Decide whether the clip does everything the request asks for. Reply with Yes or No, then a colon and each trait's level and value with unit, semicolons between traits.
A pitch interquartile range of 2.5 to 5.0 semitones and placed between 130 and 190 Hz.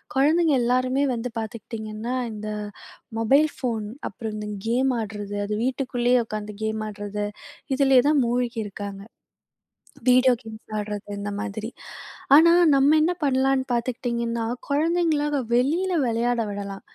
No: average, 3.9 semitones; high, 240 Hz